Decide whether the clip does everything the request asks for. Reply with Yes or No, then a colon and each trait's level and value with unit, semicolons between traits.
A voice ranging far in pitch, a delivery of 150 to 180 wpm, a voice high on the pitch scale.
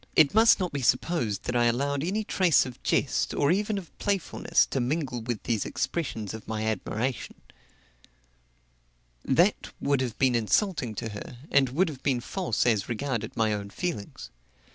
No: wide, 6.5 semitones; average, 165 wpm; low, 130 Hz